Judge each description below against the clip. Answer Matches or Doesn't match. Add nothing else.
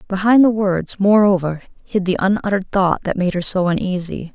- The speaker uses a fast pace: Doesn't match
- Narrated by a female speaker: Matches